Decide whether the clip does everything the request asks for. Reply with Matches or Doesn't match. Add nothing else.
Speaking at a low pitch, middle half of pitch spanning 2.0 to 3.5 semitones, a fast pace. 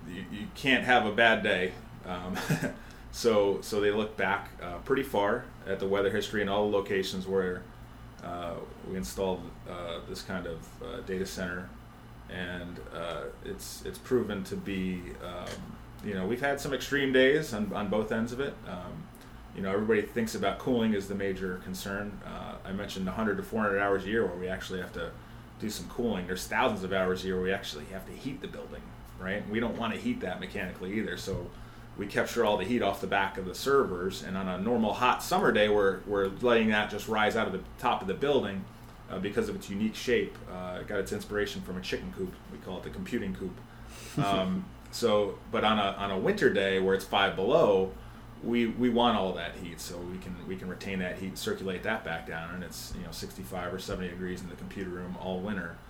Matches